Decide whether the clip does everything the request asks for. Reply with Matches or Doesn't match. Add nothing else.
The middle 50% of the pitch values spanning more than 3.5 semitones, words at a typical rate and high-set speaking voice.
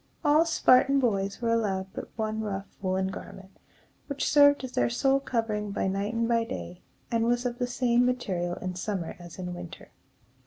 Matches